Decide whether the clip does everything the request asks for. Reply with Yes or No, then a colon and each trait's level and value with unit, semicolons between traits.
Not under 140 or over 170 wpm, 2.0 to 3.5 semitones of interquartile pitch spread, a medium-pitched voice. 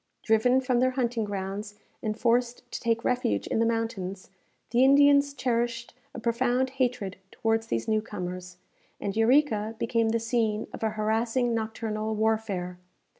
No: average, 150 wpm; narrow, 2.4 semitones; high, 225 Hz